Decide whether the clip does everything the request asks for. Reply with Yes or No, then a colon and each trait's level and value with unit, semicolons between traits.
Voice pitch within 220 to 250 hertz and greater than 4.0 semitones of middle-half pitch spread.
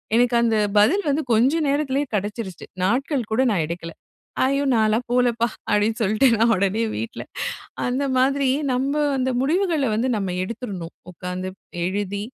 Yes: high, 230 Hz; average, 4.6 semitones